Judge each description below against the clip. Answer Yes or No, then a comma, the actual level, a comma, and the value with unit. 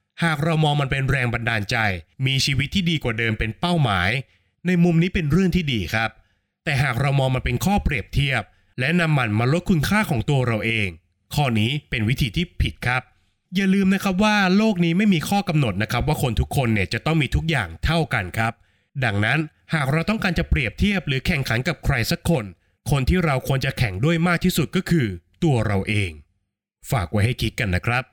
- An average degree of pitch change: No, wide, 7.1 semitones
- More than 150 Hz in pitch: No, low, 135 Hz